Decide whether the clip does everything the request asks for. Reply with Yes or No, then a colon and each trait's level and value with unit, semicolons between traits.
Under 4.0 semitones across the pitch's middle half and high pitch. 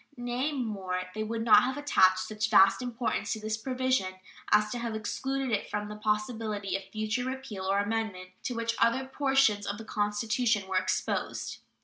Yes: average, 3.0 semitones; high, 220 Hz